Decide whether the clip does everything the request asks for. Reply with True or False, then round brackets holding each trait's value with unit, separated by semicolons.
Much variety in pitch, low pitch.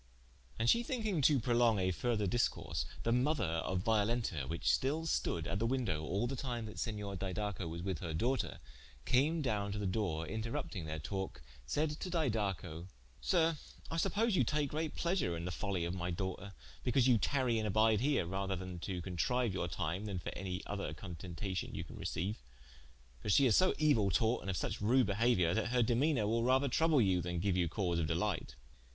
True (5.8 semitones; 105 Hz)